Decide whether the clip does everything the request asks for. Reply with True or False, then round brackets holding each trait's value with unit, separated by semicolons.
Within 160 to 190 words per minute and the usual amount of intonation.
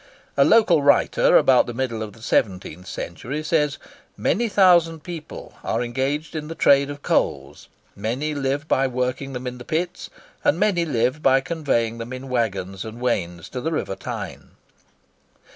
True (170 wpm; 4.8 semitones)